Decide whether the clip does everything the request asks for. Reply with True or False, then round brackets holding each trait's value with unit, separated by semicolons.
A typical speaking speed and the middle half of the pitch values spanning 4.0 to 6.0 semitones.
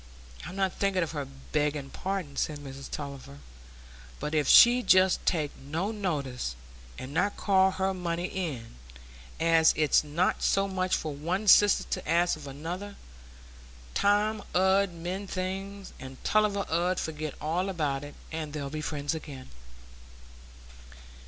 True (145 wpm; 4.5 semitones)